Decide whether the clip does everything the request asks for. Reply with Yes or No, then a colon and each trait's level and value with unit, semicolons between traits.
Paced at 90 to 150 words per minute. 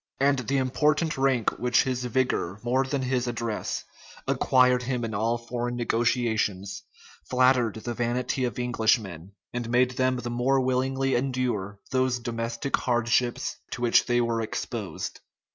Yes: average, 145 wpm